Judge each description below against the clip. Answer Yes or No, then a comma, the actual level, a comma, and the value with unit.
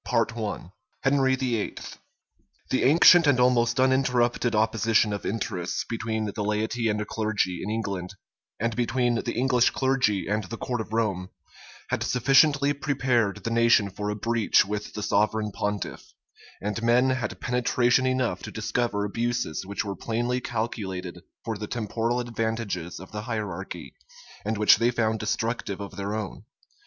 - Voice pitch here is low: Yes, low, 115 Hz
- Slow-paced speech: No, average, 155 wpm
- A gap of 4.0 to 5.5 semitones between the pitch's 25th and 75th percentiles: No, average, 2.8 semitones